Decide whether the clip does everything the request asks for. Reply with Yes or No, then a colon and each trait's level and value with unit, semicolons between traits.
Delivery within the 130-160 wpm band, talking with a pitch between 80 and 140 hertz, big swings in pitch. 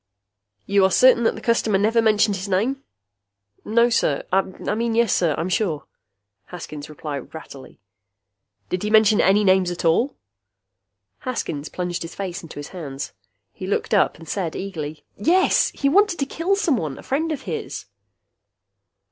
No: average, 155 wpm; high, 195 Hz; wide, 5.9 semitones